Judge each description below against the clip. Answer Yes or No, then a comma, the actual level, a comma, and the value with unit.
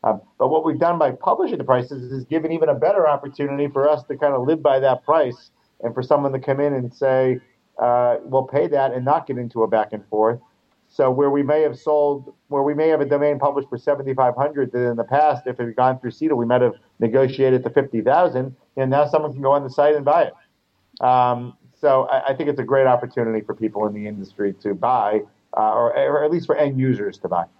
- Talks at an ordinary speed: No, fast, 250 wpm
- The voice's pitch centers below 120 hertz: No, low, 135 Hz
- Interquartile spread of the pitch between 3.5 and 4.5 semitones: No, average, 3.0 semitones